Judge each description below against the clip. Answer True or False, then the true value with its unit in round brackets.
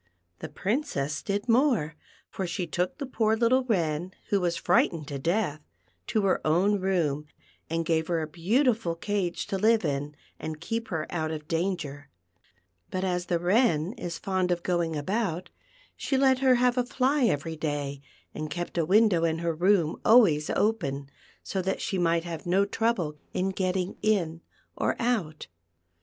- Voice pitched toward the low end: False (180 Hz)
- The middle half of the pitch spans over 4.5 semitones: True (5.1 semitones)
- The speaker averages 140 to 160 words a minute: False (170 wpm)